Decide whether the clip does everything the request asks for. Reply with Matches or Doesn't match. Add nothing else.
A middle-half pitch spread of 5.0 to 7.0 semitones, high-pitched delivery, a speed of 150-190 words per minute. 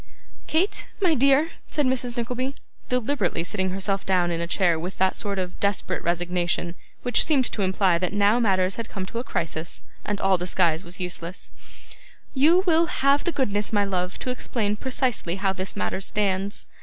Matches